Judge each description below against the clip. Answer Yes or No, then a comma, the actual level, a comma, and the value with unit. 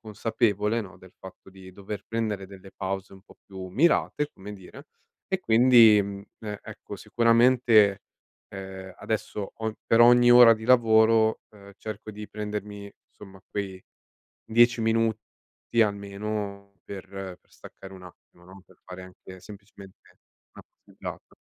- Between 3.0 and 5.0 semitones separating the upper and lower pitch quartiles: No, narrow, 2.6 semitones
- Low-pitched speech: Yes, low, 105 Hz